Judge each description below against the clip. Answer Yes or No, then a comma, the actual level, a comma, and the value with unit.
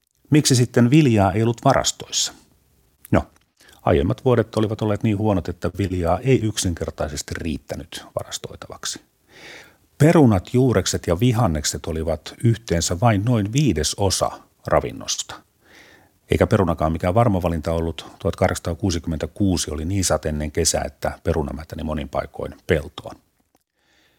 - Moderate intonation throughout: No, wide, 5.9 semitones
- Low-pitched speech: Yes, very low, 95 Hz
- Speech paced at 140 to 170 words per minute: No, average, 115 wpm